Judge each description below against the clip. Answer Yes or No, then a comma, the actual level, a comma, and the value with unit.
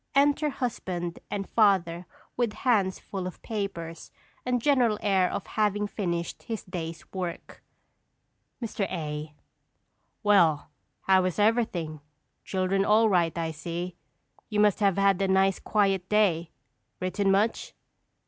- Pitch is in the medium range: No, high, 195 Hz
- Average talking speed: No, slow, 130 wpm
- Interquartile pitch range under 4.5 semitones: Yes, average, 3.4 semitones